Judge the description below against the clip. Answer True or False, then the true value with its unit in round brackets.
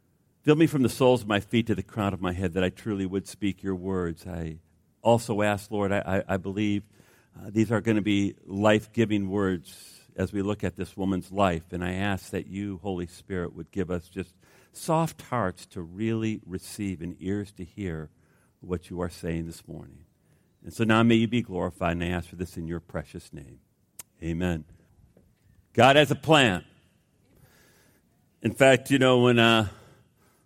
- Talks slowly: False (195 wpm)